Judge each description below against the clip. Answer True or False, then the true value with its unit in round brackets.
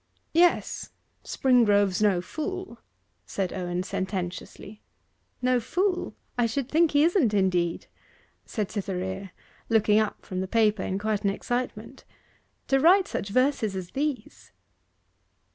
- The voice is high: True (215 Hz)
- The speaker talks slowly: True (125 wpm)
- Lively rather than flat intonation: True (6.0 semitones)